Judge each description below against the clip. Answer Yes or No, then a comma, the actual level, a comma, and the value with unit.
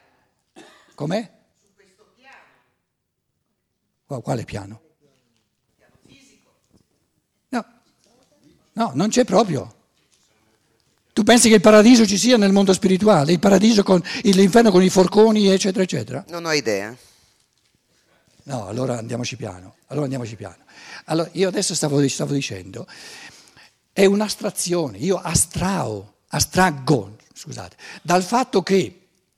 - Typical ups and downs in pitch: No, wide, 7.4 semitones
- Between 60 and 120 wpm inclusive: Yes, slow, 115 wpm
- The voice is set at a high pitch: No, medium, 180 Hz